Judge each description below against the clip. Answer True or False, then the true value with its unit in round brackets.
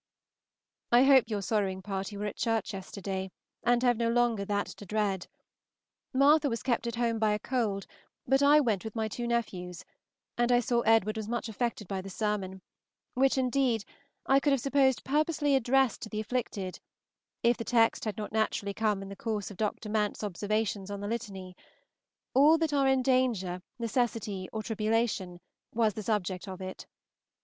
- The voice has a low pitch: False (220 Hz)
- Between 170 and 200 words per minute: True (180 wpm)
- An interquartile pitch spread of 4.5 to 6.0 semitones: False (3.4 semitones)